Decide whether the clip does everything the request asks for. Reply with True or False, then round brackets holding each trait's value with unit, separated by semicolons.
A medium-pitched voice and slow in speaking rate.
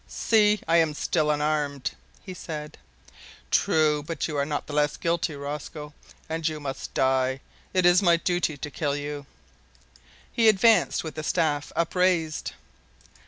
False (155 Hz; 155 wpm)